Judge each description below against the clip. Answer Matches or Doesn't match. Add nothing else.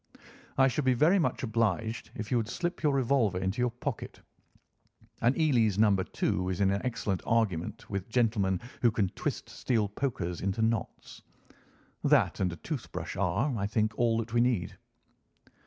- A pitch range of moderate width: Matches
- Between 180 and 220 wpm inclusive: Doesn't match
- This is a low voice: Matches